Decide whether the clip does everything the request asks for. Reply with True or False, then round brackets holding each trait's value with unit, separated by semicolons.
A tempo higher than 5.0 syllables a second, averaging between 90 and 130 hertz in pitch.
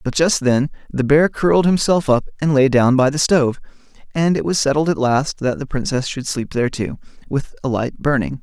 False (5.4 syllables/s; 140 Hz)